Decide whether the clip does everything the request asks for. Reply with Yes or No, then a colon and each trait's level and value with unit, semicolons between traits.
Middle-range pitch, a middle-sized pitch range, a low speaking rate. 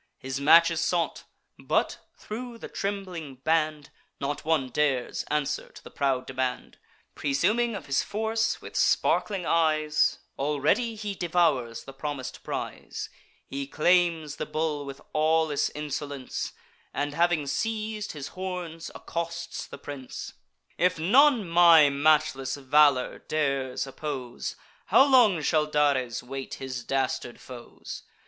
Yes: medium, 150 Hz; average, 4.1 semitones; slow, 125 wpm